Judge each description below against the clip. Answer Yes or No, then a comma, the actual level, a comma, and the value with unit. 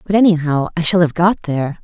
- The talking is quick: Yes, fast, 230 wpm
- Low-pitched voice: No, medium, 170 Hz